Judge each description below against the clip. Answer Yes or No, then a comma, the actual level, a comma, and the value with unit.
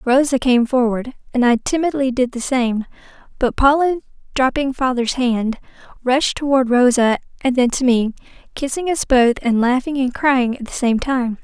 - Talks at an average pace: Yes, average, 170 wpm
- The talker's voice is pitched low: No, very high, 255 Hz